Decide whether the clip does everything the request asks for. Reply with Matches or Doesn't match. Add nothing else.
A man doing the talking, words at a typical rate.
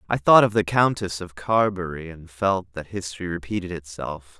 Matches